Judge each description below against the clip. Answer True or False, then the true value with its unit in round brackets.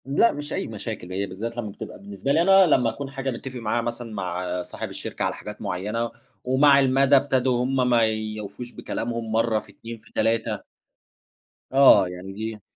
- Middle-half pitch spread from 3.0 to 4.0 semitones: True (3.7 semitones)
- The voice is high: False (115 Hz)